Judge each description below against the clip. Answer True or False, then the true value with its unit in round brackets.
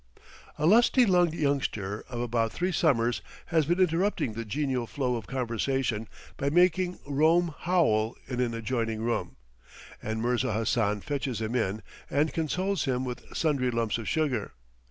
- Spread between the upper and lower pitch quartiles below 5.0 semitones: False (5.6 semitones)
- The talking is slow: False (155 wpm)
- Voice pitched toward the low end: True (130 Hz)